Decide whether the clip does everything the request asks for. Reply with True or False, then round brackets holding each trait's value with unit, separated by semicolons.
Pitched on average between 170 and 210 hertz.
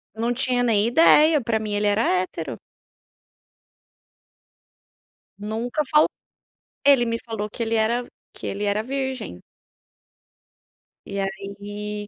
False (220 Hz)